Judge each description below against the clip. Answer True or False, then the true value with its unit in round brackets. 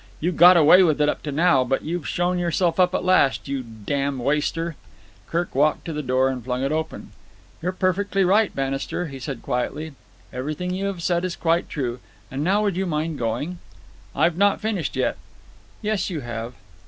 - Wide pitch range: False (4.8 semitones)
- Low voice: False (160 Hz)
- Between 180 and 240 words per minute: True (190 wpm)